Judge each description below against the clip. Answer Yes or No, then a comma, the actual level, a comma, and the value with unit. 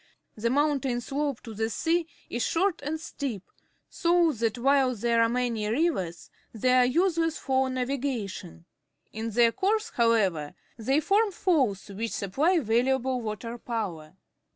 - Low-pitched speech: No, very high, 250 Hz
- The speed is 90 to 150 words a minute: Yes, average, 140 wpm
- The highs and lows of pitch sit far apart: No, average, 4.9 semitones